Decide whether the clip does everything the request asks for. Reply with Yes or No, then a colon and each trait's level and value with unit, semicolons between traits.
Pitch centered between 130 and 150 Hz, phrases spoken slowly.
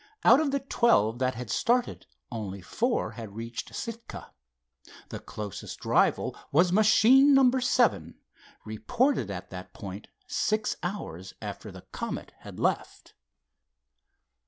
Yes: medium, 140 Hz; slow, 125 wpm